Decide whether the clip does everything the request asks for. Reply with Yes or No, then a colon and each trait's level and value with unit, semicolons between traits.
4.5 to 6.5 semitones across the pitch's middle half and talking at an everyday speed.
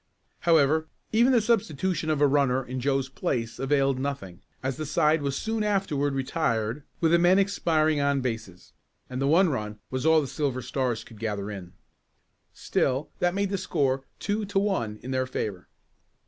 Yes: average, 4.8 semitones; average, 175 wpm